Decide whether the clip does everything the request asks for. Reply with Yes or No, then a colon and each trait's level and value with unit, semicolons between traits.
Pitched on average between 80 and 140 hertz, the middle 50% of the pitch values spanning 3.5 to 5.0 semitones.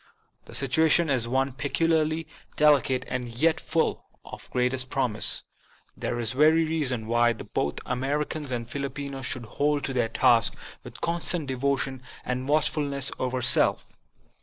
No: low, 135 Hz; average, 3.1 semitones